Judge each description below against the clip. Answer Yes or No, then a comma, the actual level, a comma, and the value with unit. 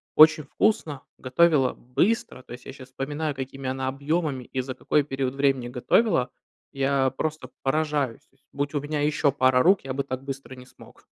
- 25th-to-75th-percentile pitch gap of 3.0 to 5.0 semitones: No, narrow, 2.5 semitones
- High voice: No, low, 135 Hz